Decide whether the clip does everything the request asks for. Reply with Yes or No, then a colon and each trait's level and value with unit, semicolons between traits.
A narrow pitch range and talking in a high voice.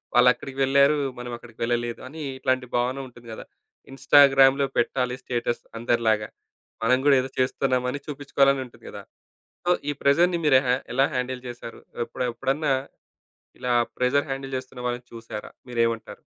No: narrow, 2.1 semitones; low, 130 Hz